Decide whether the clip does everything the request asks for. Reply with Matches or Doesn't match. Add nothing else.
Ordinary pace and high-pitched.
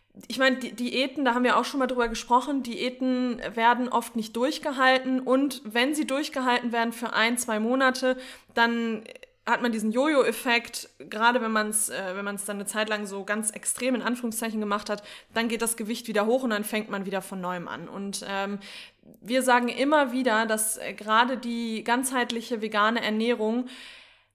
Matches